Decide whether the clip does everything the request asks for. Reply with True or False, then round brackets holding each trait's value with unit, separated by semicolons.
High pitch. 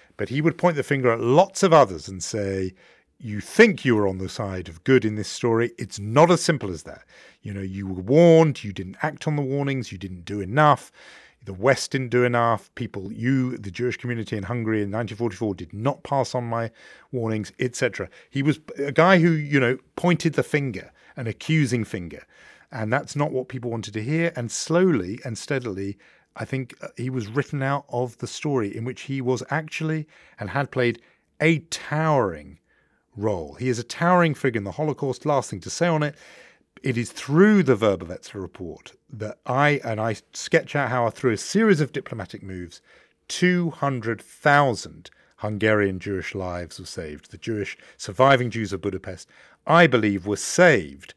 False (125 Hz)